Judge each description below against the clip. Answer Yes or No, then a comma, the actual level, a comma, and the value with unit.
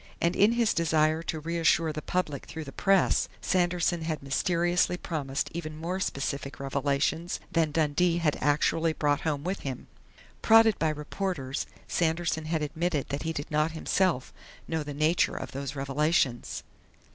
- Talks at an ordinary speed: Yes, average, 155 wpm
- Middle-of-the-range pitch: Yes, medium, 160 Hz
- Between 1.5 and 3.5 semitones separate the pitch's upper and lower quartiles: Yes, average, 2.9 semitones